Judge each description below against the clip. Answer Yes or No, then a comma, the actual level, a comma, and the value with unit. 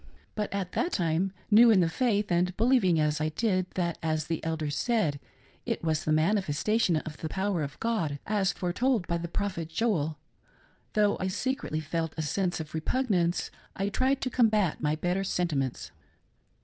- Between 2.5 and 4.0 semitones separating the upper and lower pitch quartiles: No, average, 4.9 semitones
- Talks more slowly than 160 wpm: No, average, 175 wpm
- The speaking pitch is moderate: Yes, medium, 180 Hz